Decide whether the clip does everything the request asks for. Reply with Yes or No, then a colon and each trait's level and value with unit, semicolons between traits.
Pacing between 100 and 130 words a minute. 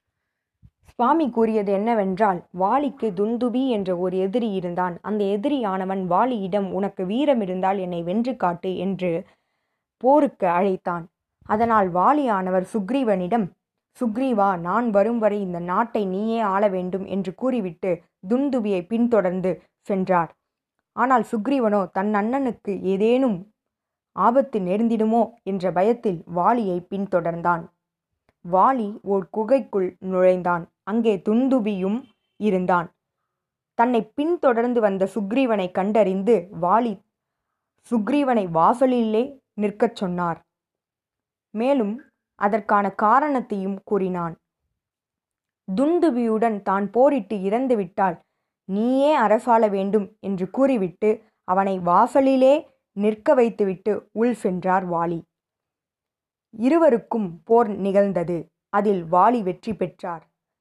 No: average, 90 wpm